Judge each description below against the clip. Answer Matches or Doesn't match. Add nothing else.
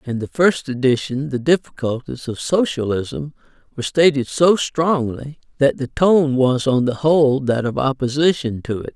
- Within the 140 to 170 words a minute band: Matches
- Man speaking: Matches